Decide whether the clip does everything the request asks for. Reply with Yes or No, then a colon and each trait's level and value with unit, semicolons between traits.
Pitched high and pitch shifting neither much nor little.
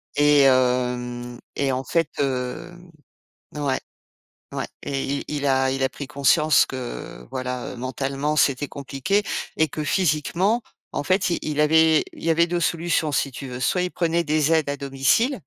No: medium, 140 Hz; average, 3.5 semitones